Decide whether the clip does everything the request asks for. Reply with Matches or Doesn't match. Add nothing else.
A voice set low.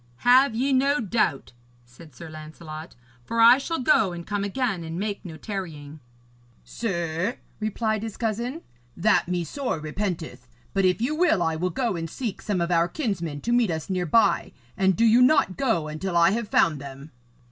Doesn't match